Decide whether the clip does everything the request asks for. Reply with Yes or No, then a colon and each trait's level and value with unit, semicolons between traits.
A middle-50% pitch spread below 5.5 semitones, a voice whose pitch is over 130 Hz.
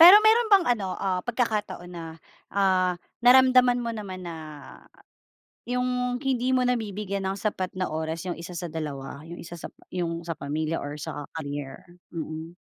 No: wide, 7.0 semitones; medium, 185 Hz